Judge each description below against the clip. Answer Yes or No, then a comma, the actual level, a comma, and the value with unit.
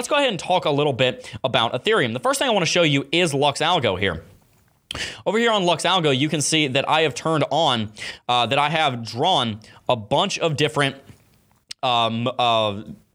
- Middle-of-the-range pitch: Yes, medium, 145 Hz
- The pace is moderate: No, fast, 210 wpm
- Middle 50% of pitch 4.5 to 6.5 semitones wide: Yes, average, 5.3 semitones